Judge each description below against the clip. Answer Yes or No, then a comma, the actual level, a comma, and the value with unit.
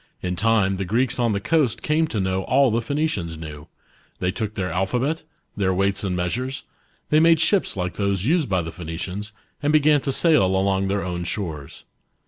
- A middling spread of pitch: No, wide, 6.6 semitones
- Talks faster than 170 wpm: Yes, average, 195 wpm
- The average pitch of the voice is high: No, low, 100 Hz